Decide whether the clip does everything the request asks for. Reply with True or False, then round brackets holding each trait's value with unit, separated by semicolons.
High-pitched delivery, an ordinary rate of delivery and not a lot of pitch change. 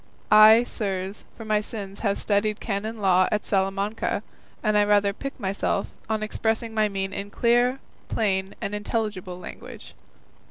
True (210 Hz; 150 wpm; 2.0 semitones)